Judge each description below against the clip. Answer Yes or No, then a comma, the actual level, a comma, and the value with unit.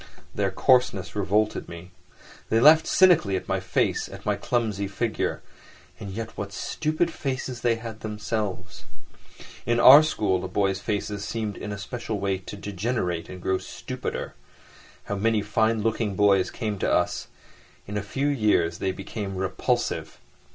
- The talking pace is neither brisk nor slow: Yes, average, 155 wpm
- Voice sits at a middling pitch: No, low, 105 Hz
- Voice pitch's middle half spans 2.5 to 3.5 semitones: Yes, average, 3.0 semitones